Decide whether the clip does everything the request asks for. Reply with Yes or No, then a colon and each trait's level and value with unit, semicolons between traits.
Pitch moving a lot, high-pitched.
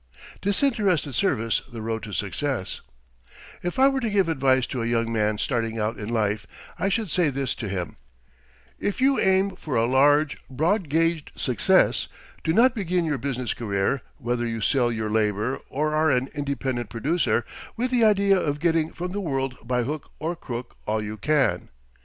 No: wide, 7.2 semitones; low, 135 Hz